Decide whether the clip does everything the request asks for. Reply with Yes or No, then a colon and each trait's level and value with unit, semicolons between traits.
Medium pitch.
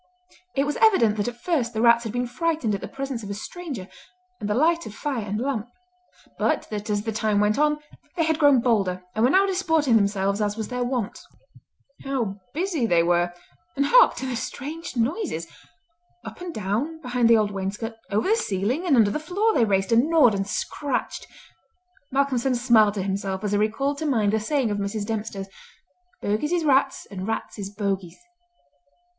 No: high, 230 Hz